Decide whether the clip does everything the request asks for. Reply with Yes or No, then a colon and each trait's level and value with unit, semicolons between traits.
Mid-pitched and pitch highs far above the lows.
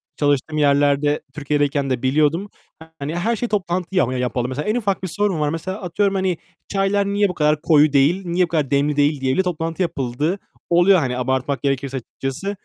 No: medium, 155 Hz; average, 5.0 semitones